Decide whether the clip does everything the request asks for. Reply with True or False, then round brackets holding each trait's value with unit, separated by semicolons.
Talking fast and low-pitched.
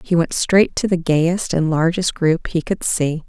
False (220 wpm; 170 Hz)